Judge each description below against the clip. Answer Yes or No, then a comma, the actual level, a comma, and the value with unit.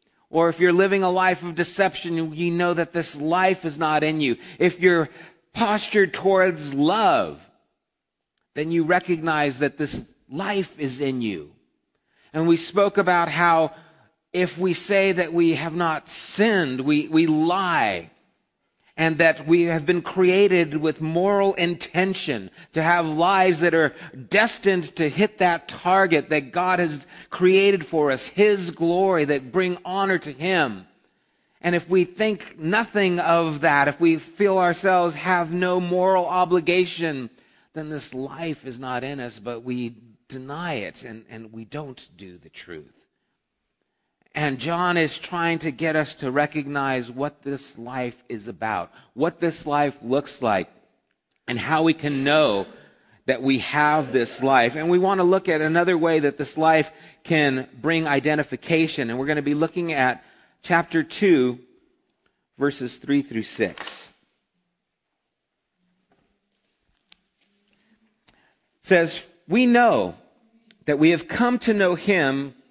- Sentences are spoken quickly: No, average, 150 wpm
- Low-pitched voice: No, medium, 165 Hz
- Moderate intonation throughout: Yes, average, 3.8 semitones